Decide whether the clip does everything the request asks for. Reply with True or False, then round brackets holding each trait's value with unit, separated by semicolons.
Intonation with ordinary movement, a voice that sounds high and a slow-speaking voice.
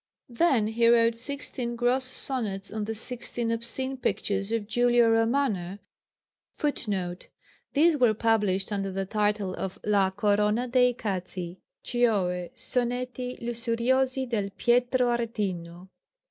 True (3.6 semitones; 230 Hz; 120 wpm)